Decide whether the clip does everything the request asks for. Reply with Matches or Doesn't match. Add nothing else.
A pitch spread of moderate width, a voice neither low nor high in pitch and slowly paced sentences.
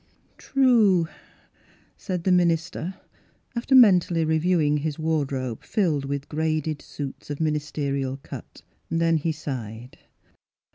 Matches